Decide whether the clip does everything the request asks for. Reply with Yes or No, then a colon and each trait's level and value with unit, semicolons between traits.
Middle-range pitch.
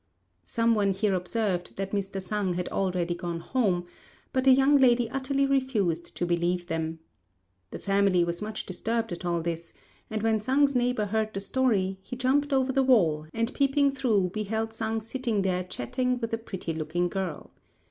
No: high, 210 Hz